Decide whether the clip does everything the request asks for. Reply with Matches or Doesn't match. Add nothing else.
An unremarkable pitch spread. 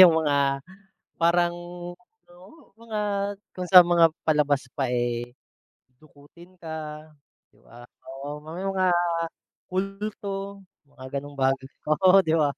Matches